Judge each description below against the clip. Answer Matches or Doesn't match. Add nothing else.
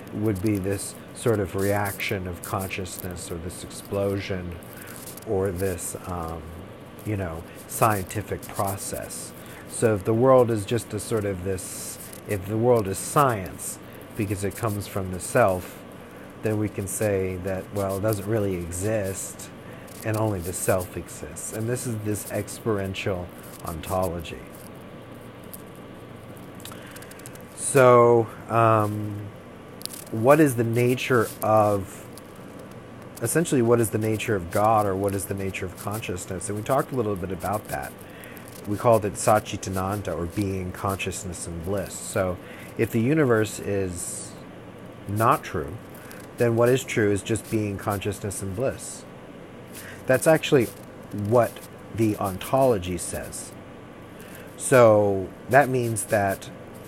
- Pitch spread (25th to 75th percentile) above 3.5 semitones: Doesn't match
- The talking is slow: Matches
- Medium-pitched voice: Doesn't match